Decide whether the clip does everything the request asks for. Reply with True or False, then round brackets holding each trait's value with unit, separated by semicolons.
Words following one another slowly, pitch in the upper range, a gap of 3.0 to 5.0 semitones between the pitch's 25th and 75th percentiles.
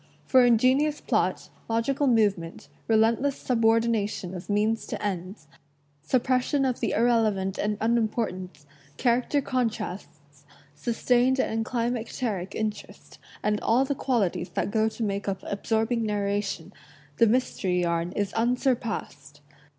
True (125 wpm; 220 Hz; 3.6 semitones)